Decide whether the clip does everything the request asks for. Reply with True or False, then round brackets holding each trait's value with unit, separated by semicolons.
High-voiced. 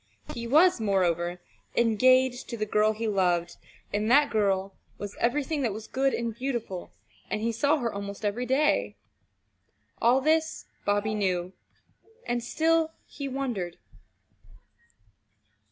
True (230 Hz)